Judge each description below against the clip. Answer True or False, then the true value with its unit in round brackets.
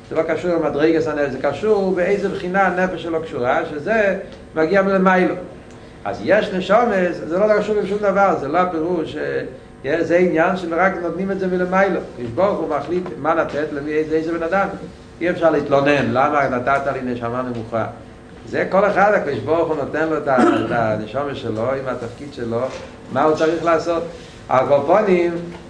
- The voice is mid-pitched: True (165 Hz)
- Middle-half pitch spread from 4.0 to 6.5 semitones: True (4.5 semitones)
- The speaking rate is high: True (155 wpm)